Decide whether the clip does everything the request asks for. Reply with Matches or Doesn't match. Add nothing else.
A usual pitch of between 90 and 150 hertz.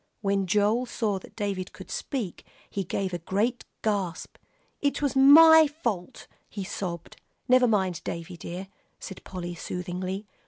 Doesn't match